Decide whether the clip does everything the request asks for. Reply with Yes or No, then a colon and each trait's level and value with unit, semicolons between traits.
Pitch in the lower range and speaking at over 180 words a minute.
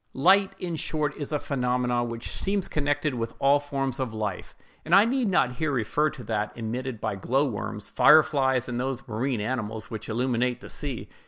Yes: low, 130 Hz; average, 190 wpm